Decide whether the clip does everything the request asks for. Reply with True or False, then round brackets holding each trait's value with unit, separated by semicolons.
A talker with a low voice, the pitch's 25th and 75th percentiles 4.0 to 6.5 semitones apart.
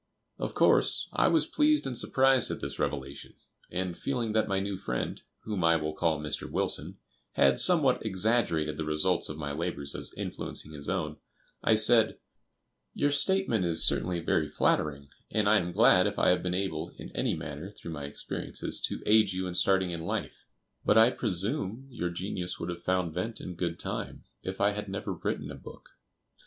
True (90 Hz; 5.0 semitones)